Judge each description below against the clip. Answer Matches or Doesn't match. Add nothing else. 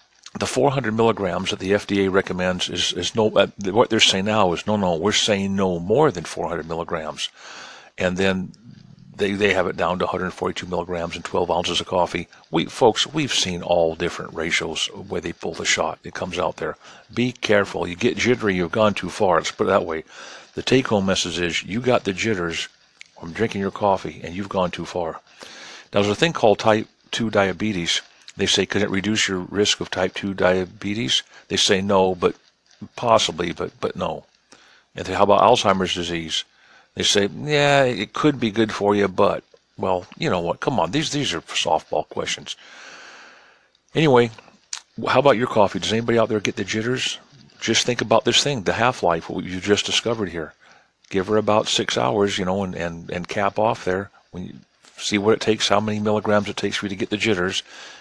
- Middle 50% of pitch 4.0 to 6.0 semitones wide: Doesn't match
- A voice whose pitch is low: Matches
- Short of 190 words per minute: Doesn't match